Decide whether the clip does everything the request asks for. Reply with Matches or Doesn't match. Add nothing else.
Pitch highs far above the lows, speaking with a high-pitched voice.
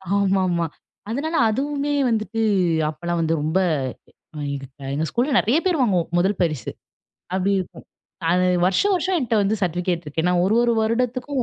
Matches